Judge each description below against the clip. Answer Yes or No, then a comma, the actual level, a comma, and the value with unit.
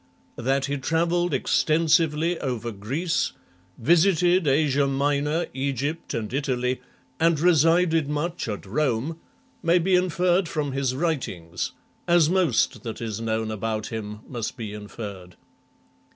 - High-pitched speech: No, medium, 140 Hz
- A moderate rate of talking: No, slow, 125 wpm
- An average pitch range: No, wide, 6.3 semitones